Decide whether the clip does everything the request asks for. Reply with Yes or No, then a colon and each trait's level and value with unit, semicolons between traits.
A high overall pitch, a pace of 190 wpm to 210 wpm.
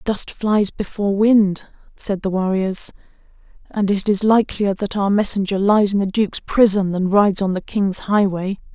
No: high, 200 Hz; average, 170 wpm